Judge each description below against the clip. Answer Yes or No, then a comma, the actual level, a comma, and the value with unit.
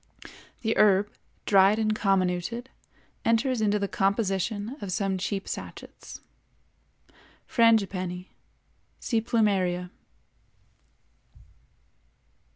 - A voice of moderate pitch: No, high, 200 Hz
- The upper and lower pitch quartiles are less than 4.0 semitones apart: Yes, average, 2.8 semitones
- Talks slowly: Yes, slow, 75 wpm